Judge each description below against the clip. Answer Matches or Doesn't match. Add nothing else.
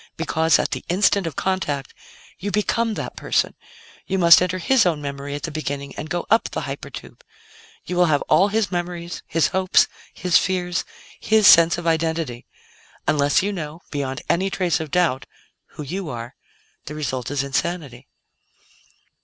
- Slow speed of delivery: Doesn't match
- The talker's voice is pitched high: Doesn't match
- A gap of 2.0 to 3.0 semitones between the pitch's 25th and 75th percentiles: Doesn't match